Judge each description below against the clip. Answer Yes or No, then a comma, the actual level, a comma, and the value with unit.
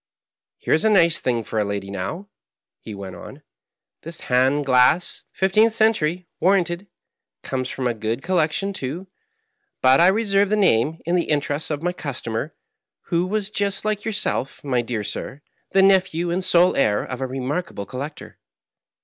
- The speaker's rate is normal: Yes, average, 170 wpm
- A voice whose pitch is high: No, medium, 155 Hz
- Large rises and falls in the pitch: Yes, wide, 6.8 semitones